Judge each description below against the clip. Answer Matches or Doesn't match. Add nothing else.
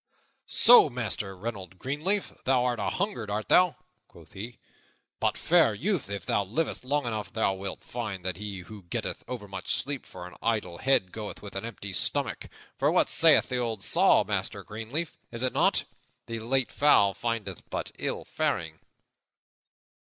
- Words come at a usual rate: Matches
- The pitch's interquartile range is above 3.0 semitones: Matches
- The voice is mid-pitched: Doesn't match